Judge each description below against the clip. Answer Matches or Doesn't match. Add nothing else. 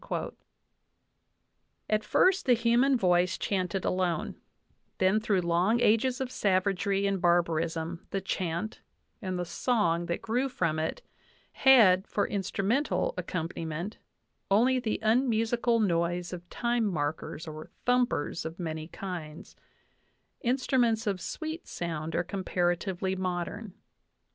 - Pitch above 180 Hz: Matches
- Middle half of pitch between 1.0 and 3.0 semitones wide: Doesn't match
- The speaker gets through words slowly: Matches